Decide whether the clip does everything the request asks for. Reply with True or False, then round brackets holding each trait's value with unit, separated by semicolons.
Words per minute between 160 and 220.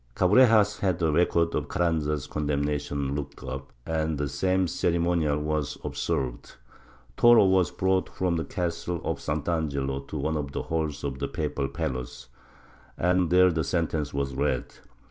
False (150 wpm)